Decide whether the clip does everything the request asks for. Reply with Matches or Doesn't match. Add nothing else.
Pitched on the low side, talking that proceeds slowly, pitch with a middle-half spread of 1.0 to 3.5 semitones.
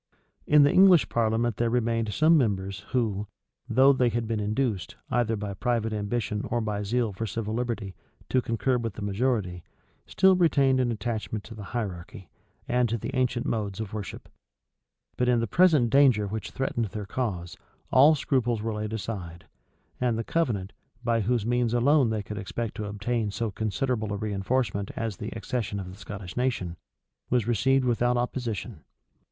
Doesn't match